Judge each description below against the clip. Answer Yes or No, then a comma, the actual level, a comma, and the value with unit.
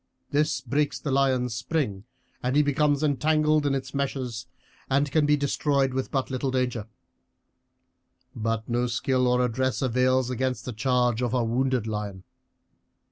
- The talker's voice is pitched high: No, low, 130 Hz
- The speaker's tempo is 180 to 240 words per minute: No, average, 145 wpm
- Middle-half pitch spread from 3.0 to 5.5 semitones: No, narrow, 2.4 semitones